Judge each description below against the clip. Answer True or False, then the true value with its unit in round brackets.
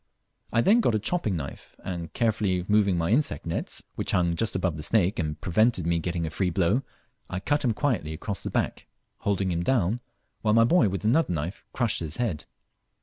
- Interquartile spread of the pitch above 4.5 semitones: True (5.1 semitones)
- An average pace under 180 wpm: False (205 wpm)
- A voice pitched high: False (95 Hz)